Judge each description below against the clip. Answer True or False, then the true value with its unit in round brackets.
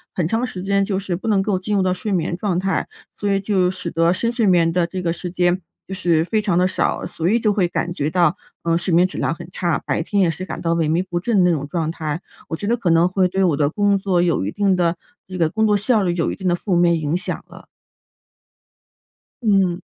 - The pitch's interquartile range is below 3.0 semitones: True (2.5 semitones)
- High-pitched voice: False (180 Hz)